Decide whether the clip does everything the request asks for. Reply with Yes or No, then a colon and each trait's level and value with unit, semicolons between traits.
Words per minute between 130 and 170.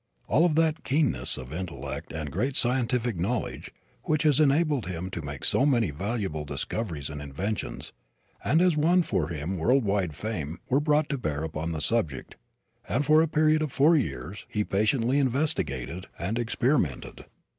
Yes: average, 165 wpm